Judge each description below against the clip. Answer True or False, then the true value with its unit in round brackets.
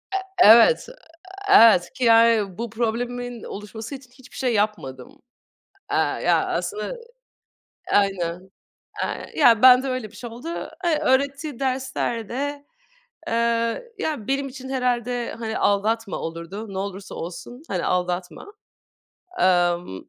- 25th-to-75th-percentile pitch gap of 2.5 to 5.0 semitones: True (4.7 semitones)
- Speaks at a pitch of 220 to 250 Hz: True (230 Hz)